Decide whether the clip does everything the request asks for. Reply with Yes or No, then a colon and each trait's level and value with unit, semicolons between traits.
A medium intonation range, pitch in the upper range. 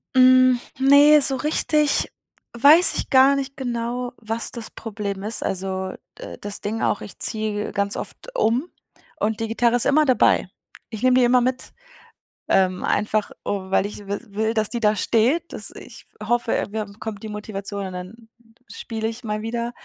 Yes: average, 3.5 semitones; high, 225 Hz